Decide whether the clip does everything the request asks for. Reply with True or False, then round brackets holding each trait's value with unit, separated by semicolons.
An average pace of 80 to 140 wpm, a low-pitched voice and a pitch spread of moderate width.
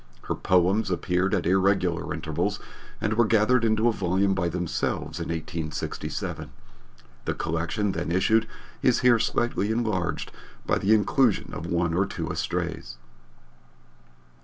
True (135 wpm; 95 Hz; 4.2 semitones)